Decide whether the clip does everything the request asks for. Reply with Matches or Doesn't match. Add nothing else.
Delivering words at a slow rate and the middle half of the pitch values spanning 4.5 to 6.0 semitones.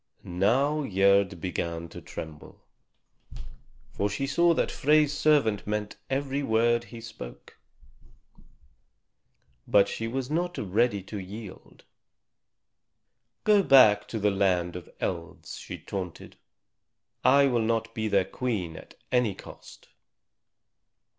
Matches